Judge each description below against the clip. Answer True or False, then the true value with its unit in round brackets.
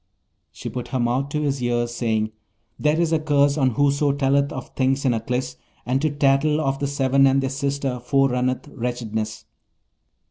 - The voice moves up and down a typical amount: False (2.3 semitones)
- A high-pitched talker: False (135 Hz)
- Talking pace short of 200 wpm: True (175 wpm)